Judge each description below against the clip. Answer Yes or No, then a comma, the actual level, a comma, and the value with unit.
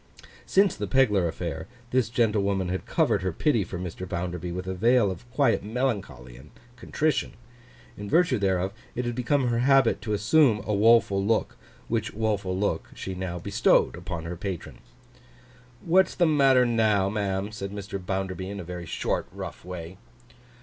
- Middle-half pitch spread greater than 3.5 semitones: Yes, average, 4.6 semitones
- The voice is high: No, low, 100 Hz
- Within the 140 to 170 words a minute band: Yes, average, 165 wpm